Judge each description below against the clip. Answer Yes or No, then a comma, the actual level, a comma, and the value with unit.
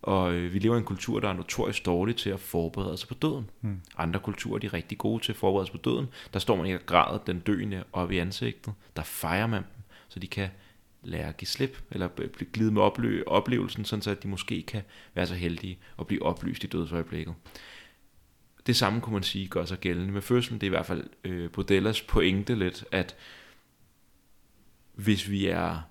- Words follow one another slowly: No, average, 210 wpm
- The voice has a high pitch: No, low, 100 Hz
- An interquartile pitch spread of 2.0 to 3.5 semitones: Yes, average, 3.2 semitones